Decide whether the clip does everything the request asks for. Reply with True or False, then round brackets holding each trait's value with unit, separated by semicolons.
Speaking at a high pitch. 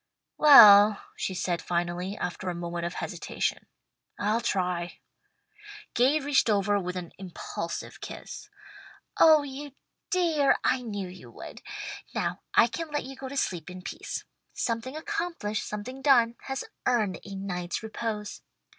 True (210 Hz)